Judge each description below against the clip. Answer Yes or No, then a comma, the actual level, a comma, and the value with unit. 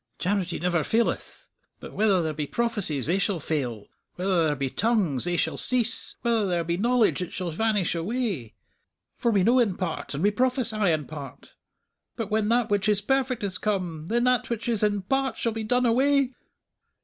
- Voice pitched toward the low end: No, high, 205 Hz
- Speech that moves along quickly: No, average, 195 wpm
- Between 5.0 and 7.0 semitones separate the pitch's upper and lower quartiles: Yes, wide, 5.5 semitones